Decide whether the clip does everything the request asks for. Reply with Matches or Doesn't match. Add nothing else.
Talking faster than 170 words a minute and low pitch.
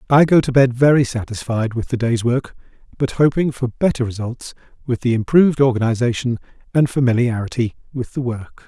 Doesn't match